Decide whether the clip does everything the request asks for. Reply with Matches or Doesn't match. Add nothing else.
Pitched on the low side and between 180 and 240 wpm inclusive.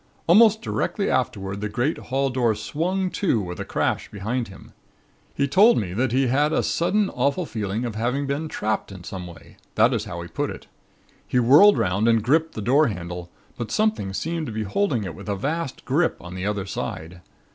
Matches